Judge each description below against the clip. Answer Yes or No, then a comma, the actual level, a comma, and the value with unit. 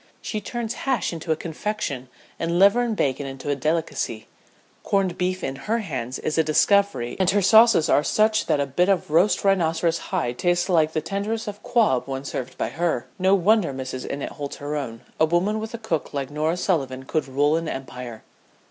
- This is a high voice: No, medium, 165 Hz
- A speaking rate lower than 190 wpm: No, average, 200 wpm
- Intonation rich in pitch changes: Yes, wide, 6.3 semitones